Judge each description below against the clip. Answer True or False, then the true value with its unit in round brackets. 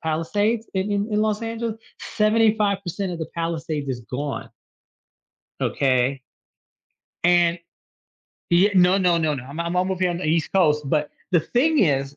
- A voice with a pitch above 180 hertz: False (175 Hz)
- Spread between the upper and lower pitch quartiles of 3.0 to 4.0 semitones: False (4.9 semitones)